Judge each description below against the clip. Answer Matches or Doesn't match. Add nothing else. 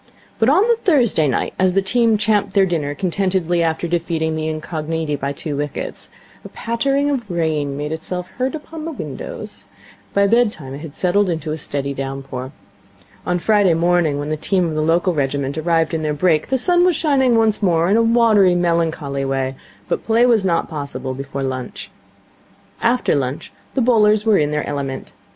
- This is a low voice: Doesn't match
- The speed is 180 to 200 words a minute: Matches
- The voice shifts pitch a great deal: Matches